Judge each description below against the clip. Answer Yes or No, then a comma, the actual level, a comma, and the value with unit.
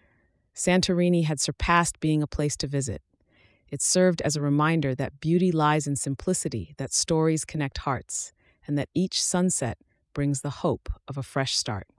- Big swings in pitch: No, average, 3.6 semitones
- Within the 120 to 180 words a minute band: Yes, average, 165 wpm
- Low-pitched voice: No, medium, 150 Hz